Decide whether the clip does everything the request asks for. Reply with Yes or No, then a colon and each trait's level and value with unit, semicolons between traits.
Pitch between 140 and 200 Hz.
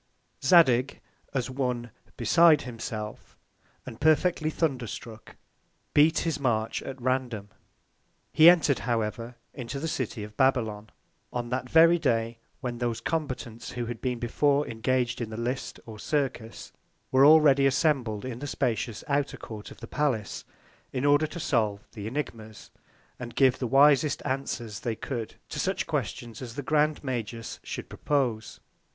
No: low, 125 Hz